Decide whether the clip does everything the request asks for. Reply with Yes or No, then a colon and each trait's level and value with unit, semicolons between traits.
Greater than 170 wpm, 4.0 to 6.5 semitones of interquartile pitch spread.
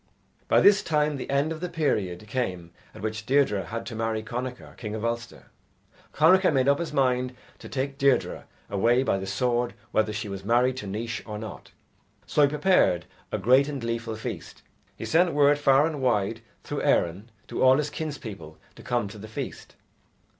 Yes: average, 190 wpm; average, 4.7 semitones